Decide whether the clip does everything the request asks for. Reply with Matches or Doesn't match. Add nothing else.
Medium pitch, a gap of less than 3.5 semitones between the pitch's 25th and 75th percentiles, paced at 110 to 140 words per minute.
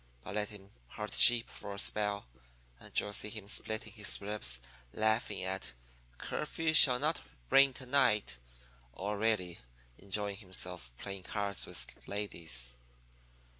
Doesn't match